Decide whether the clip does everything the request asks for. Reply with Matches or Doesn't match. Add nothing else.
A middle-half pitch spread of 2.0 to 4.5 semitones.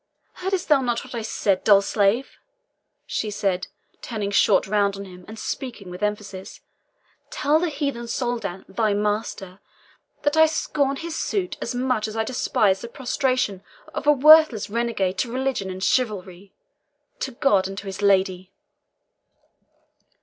Doesn't match